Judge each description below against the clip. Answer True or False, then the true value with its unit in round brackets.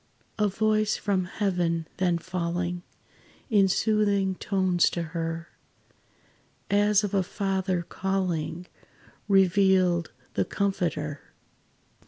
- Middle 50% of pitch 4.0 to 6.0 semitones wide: False (2.5 semitones)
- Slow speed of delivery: True (95 wpm)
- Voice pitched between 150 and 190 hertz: True (185 Hz)